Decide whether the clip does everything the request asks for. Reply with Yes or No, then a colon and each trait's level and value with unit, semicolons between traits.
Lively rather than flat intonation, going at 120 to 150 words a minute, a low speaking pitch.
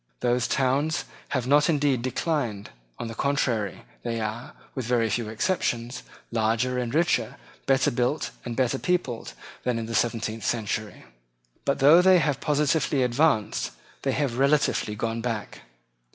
No: average, 3.7 semitones; average, 145 wpm; low, 125 Hz